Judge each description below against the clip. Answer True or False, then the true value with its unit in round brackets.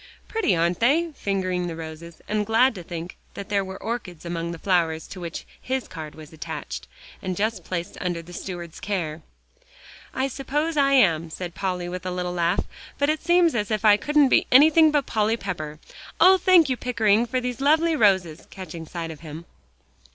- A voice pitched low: False (190 Hz)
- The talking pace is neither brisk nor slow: True (190 wpm)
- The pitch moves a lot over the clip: True (7.1 semitones)